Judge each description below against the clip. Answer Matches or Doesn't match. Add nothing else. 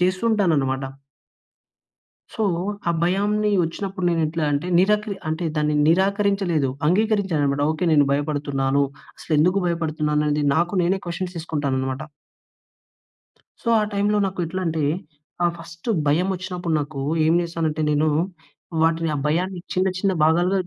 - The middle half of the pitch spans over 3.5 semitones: Matches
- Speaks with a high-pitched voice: Doesn't match